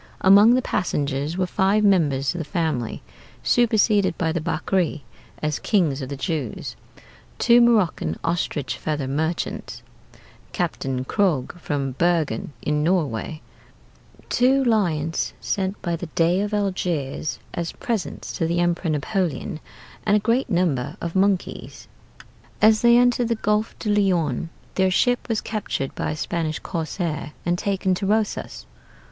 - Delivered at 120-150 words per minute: Yes, average, 140 wpm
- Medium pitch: Yes, medium, 175 Hz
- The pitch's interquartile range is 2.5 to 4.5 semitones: No, average, 5.1 semitones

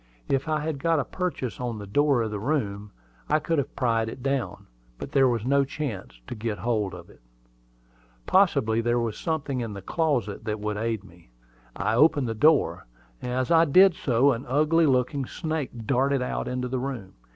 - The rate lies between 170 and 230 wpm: Yes, average, 195 wpm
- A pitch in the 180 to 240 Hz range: No, low, 125 Hz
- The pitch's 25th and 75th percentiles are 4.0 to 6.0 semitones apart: Yes, average, 4.7 semitones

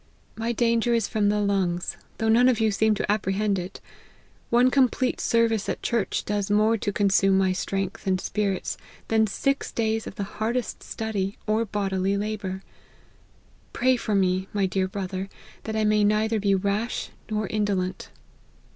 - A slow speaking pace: No, average, 165 wpm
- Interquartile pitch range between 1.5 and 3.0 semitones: Yes, narrow, 2.4 semitones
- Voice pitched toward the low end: No, high, 210 Hz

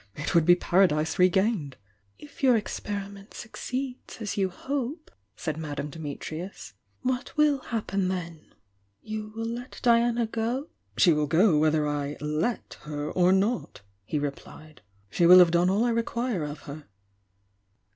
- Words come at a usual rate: Yes, average, 155 wpm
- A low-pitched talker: No, high, 190 Hz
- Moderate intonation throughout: No, wide, 7.0 semitones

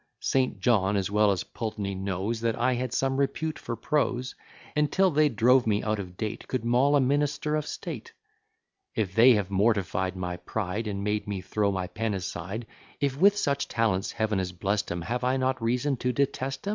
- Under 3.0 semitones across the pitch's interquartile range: No, average, 4.9 semitones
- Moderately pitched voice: No, low, 115 Hz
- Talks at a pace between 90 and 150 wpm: No, average, 200 wpm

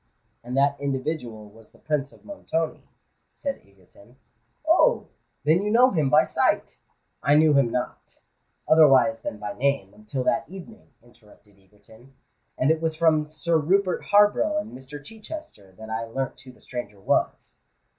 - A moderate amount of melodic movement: No, wide, 6.0 semitones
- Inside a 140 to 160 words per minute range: Yes, average, 155 wpm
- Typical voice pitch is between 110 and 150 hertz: Yes, medium, 140 Hz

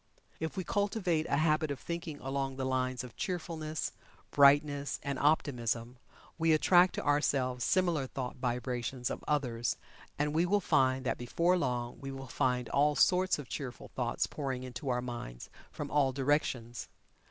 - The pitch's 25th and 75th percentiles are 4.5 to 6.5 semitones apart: No, average, 3.7 semitones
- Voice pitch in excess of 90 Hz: Yes, medium, 140 Hz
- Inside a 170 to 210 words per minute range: No, average, 160 wpm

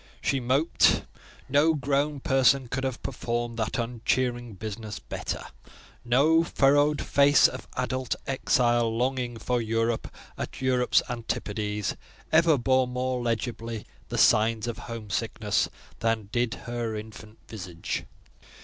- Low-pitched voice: Yes, low, 120 Hz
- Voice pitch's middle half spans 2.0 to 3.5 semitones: Yes, narrow, 2.6 semitones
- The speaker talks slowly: Yes, slow, 120 wpm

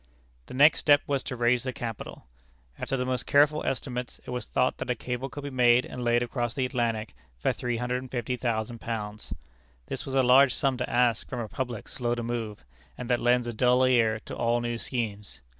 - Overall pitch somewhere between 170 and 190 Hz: No, low, 125 Hz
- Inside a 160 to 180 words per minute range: No, average, 200 wpm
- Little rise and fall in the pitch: Yes, narrow, 1.5 semitones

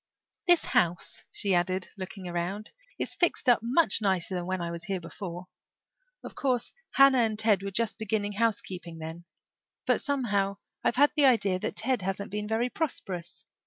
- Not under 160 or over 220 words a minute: Yes, average, 170 wpm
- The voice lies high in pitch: Yes, high, 200 Hz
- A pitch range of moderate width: Yes, average, 4.3 semitones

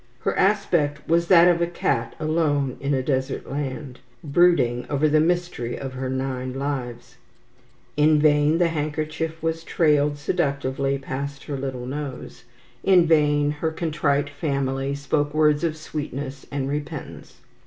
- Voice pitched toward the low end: No, medium, 145 Hz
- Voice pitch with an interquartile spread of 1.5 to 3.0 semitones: Yes, narrow, 2.5 semitones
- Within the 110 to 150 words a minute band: Yes, average, 145 wpm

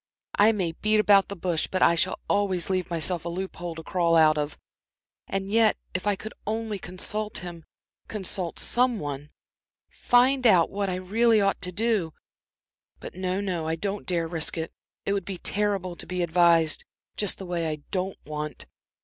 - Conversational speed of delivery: Yes, average, 185 wpm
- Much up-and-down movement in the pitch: No, average, 3.4 semitones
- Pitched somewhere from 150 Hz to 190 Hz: Yes, medium, 185 Hz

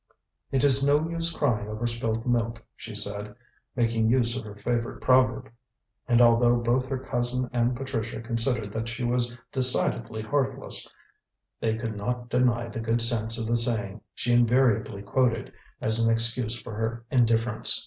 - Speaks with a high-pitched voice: No, low, 120 Hz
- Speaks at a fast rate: No, average, 160 wpm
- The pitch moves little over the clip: Yes, narrow, 1.8 semitones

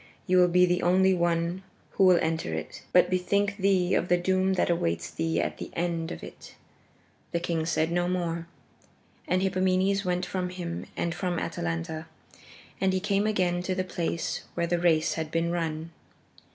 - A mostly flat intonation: Yes, narrow, 1.8 semitones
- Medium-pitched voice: Yes, medium, 175 Hz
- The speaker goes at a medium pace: Yes, average, 180 wpm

